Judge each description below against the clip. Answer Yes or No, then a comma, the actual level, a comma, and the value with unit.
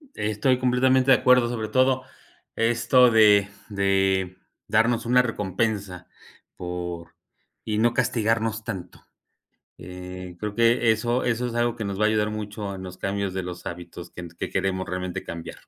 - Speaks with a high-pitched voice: No, low, 105 Hz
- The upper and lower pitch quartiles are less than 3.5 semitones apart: No, average, 4.2 semitones